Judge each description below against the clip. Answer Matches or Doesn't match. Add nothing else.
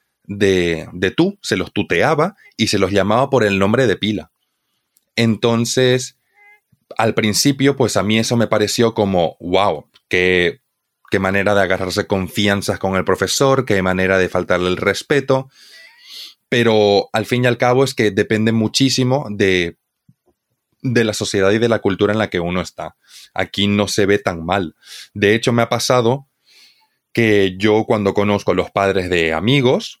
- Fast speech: Doesn't match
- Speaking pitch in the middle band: Doesn't match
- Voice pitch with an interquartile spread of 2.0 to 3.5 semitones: Doesn't match